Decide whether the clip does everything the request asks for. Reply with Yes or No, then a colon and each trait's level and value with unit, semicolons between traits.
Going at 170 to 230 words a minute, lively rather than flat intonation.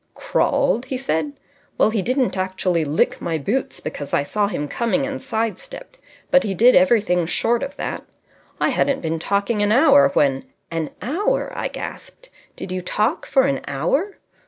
Yes: average, 180 wpm; wide, 7.7 semitones